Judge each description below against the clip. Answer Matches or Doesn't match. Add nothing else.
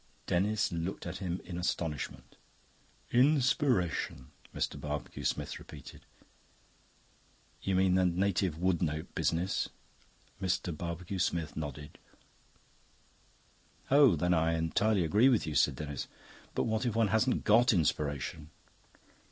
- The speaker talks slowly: Matches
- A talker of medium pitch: Doesn't match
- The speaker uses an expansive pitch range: Doesn't match